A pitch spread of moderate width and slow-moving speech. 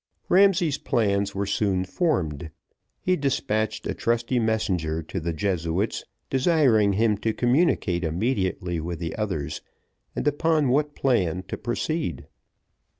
No: wide, 7.0 semitones; slow, 125 wpm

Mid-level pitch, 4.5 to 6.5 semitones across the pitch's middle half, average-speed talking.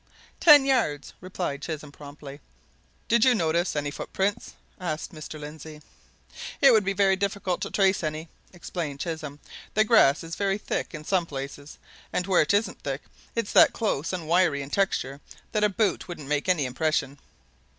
Yes: medium, 170 Hz; average, 5.1 semitones; average, 165 wpm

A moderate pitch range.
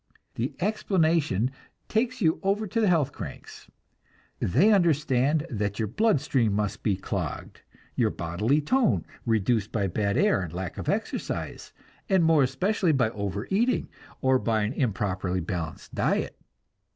No: wide, 9.0 semitones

